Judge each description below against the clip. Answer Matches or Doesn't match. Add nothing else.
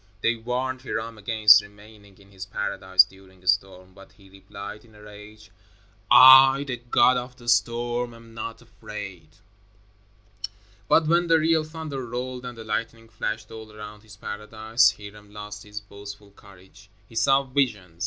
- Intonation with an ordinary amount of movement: Matches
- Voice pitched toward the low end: Matches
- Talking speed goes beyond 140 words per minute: Matches